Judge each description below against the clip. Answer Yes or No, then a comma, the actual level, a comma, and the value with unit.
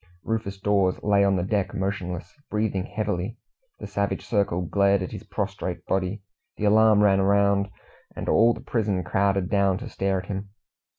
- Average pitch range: No, narrow, 1.4 semitones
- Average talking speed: Yes, average, 170 wpm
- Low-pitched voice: Yes, low, 100 Hz